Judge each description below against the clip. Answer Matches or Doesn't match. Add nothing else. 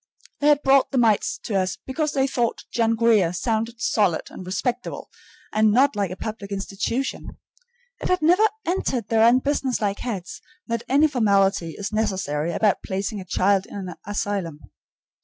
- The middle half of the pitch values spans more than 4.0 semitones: Matches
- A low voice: Doesn't match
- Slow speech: Doesn't match